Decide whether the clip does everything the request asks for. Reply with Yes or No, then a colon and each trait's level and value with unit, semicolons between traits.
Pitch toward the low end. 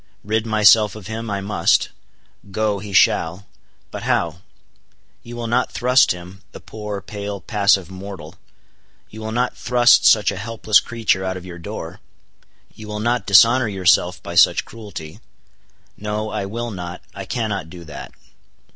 Yes: low, 105 Hz